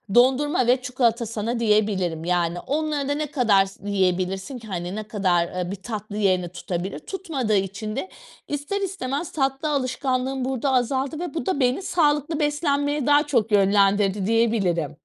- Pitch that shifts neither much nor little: No, wide, 6.5 semitones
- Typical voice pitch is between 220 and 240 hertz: Yes, high, 235 Hz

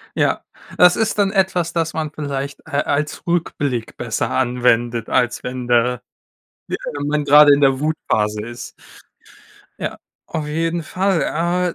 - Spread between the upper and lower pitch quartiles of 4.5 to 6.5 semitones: Yes, average, 5.1 semitones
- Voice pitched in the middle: Yes, medium, 145 Hz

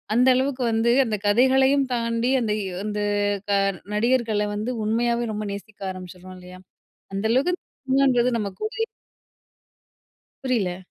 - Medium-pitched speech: No, high, 230 Hz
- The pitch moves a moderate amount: Yes, average, 3.7 semitones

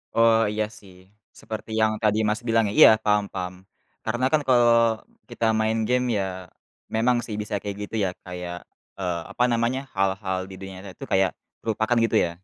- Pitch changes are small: No, average, 3.0 semitones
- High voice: No, low, 105 Hz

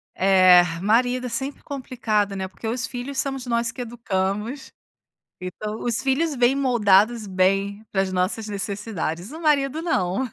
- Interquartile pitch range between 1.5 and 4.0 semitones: No, average, 4.7 semitones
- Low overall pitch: No, high, 225 Hz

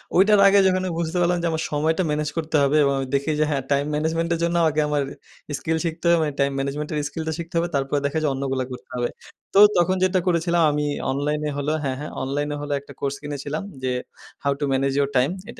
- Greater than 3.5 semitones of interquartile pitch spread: No, average, 3.1 semitones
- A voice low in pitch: No, medium, 150 Hz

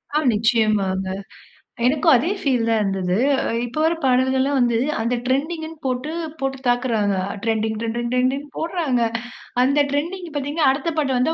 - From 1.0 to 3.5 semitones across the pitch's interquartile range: No, average, 4.1 semitones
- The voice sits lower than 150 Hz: No, very high, 255 Hz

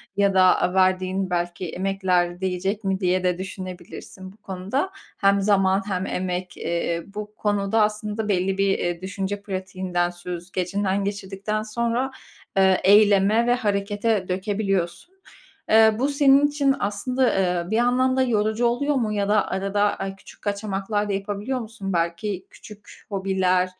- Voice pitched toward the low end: No, high, 195 Hz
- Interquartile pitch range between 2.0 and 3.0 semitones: Yes, narrow, 2.4 semitones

